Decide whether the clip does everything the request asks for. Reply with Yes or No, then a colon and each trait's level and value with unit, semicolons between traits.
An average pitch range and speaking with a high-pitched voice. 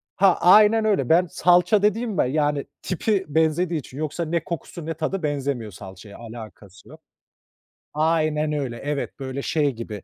No: average, 4.7 semitones; medium, 155 Hz